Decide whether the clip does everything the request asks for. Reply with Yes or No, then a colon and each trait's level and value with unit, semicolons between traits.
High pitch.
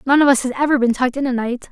Yes: very high, 260 Hz